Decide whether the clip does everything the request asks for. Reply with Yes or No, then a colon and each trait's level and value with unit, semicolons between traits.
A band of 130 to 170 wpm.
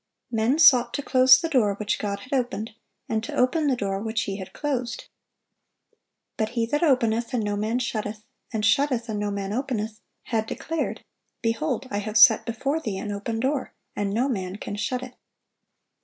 No: average, 185 wpm